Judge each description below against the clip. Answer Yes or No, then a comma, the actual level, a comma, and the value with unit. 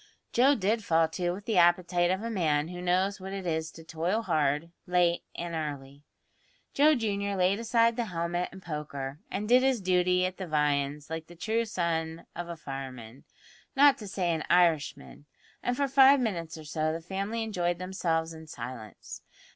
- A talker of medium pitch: Yes, medium, 175 Hz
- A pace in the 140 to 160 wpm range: No, average, 185 wpm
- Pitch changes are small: No, average, 4.0 semitones